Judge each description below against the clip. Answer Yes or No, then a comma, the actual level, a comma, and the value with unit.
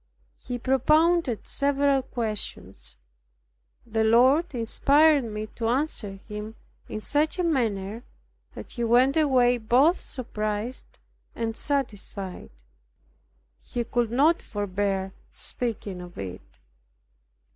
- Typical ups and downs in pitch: Yes, average, 4.6 semitones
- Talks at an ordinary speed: No, slow, 105 wpm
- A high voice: Yes, high, 240 Hz